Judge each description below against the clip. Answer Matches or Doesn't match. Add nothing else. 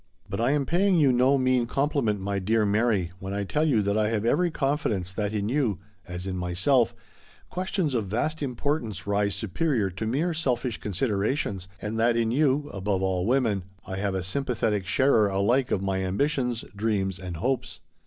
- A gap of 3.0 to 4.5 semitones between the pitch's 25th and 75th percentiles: Doesn't match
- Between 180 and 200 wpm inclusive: Matches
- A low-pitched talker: Matches